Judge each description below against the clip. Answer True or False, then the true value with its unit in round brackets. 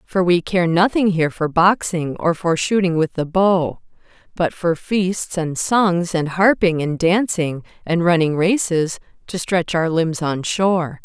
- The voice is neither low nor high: True (175 Hz)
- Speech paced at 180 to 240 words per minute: False (170 wpm)